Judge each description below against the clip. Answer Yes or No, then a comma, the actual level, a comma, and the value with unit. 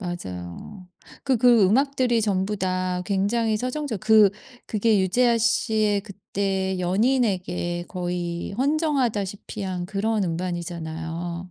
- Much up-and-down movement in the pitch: No, average, 4.0 semitones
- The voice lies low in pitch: No, high, 195 Hz